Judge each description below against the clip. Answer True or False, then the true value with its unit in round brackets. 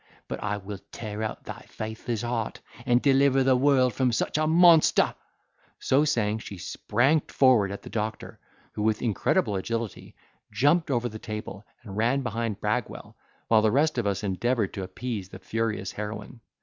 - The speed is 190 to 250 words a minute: False (170 wpm)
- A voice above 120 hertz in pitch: False (115 Hz)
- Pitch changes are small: False (3.6 semitones)